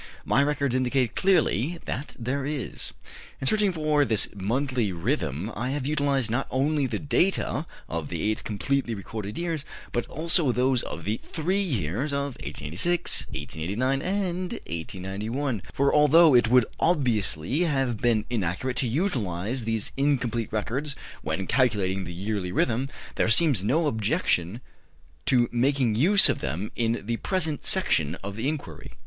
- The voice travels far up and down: Yes, wide, 5.7 semitones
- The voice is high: No, low, 125 Hz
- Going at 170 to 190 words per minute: No, average, 150 wpm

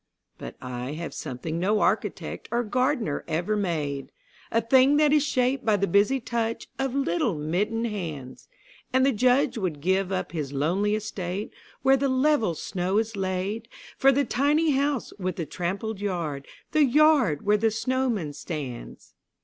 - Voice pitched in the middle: No, high, 210 Hz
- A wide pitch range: Yes, wide, 7.1 semitones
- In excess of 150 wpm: Yes, average, 160 wpm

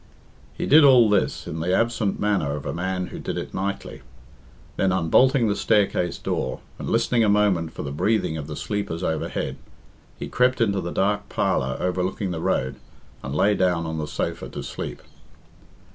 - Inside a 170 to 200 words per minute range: Yes, average, 180 wpm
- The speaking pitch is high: No, very low, 95 Hz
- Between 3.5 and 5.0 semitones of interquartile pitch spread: Yes, average, 4.3 semitones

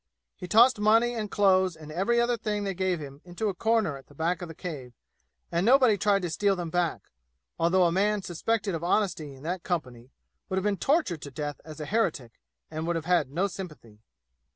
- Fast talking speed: Yes, fast, 215 wpm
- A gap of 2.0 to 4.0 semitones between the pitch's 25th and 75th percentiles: No, average, 4.8 semitones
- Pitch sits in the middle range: Yes, medium, 180 Hz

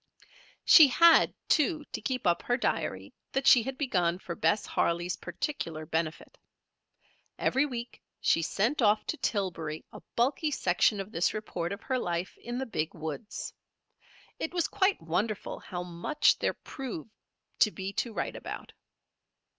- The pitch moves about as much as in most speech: No, wide, 7.5 semitones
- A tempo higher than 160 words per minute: No, average, 155 wpm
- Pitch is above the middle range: Yes, high, 210 Hz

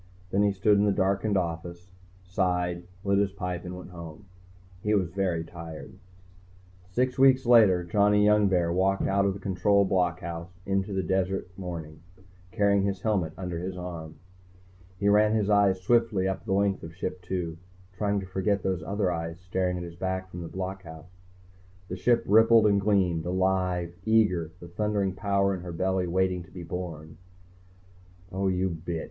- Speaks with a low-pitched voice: Yes, very low, 95 Hz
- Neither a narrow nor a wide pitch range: No, narrow, 2.3 semitones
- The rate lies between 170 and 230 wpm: Yes, average, 175 wpm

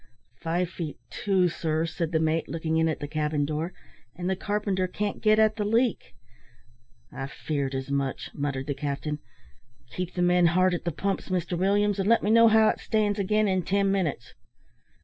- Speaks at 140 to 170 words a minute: No, average, 190 wpm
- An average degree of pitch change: Yes, average, 4.4 semitones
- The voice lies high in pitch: No, medium, 180 Hz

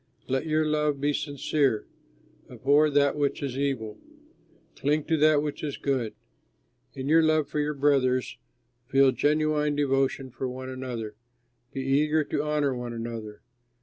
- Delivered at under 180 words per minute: Yes, average, 150 wpm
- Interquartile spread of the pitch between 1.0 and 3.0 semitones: Yes, narrow, 2.5 semitones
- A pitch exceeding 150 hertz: No, medium, 140 Hz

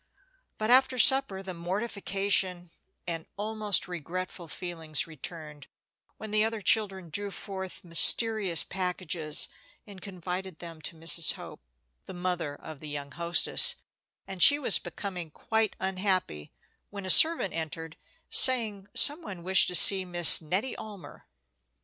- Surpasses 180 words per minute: No, slow, 135 wpm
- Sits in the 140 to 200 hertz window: Yes, medium, 185 Hz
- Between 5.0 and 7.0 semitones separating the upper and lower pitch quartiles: No, average, 3.5 semitones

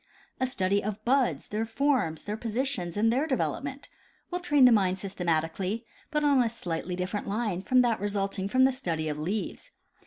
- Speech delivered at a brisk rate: No, average, 180 wpm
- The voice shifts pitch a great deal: Yes, wide, 5.7 semitones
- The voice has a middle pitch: No, high, 215 Hz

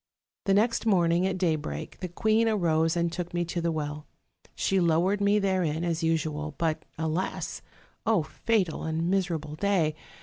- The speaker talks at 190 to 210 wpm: No, average, 155 wpm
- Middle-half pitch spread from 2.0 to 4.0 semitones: Yes, average, 3.2 semitones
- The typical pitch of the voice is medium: Yes, medium, 170 Hz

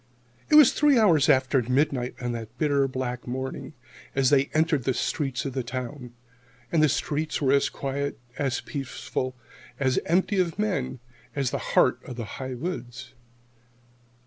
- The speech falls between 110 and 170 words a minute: Yes, average, 160 wpm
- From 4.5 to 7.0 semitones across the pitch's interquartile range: No, average, 3.2 semitones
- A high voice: No, low, 135 Hz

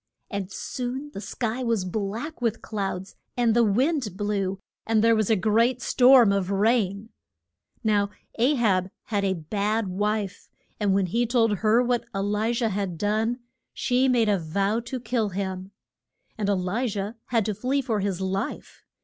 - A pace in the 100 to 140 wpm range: No, average, 175 wpm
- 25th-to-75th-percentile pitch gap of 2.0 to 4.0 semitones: Yes, average, 3.2 semitones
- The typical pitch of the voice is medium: No, high, 215 Hz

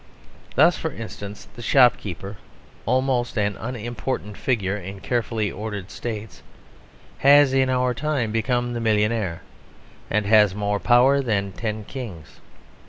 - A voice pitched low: Yes, low, 115 Hz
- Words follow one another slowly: Yes, slow, 125 wpm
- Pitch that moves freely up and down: No, average, 3.5 semitones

